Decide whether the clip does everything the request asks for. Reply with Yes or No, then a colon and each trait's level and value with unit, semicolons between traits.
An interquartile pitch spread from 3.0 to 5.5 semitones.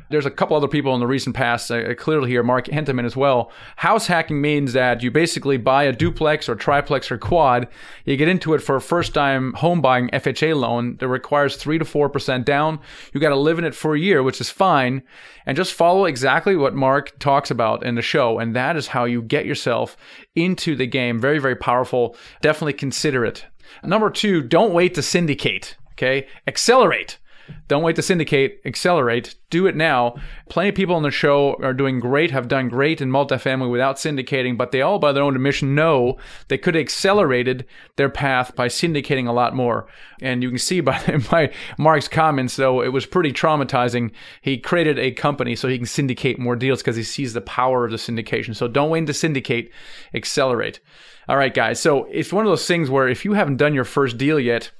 Yes: average, 3.6 semitones